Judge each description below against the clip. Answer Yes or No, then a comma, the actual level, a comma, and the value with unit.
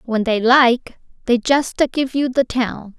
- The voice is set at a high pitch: Yes, high, 245 Hz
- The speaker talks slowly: No, average, 200 wpm